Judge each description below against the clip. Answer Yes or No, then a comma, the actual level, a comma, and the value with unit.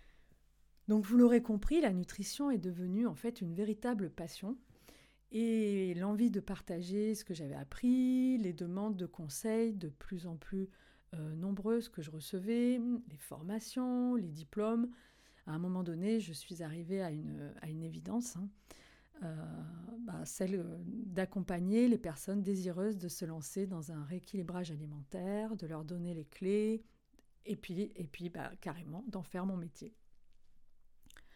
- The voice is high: Yes, high, 195 Hz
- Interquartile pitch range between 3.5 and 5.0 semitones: Yes, average, 4.3 semitones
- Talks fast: No, average, 155 wpm